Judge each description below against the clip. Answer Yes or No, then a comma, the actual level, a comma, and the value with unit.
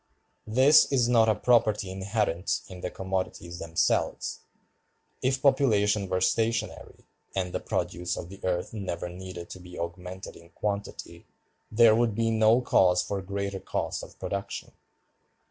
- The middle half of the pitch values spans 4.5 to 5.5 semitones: No, average, 3.7 semitones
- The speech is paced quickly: No, average, 145 wpm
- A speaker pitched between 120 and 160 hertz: No, low, 100 Hz